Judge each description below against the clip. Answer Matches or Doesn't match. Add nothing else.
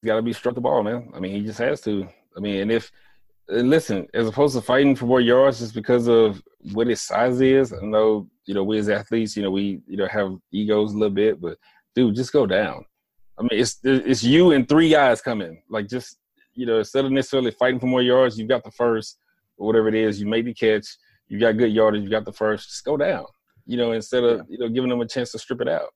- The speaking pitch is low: Matches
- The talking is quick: Matches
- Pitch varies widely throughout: Doesn't match